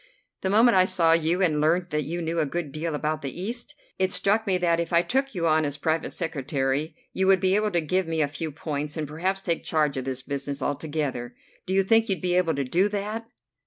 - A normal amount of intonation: Yes, average, 3.9 semitones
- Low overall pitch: No, medium, 165 Hz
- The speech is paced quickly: Yes, fast, 240 wpm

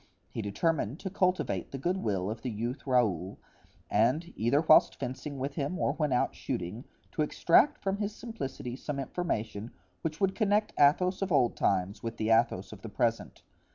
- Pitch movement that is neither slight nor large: No, wide, 7.4 semitones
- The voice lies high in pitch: No, low, 135 Hz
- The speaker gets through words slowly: No, average, 185 wpm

